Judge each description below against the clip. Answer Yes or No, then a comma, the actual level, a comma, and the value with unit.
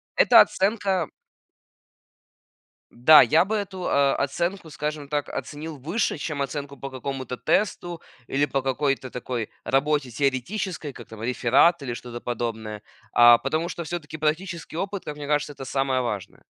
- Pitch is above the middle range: No, medium, 145 Hz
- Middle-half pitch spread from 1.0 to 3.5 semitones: No, average, 4.3 semitones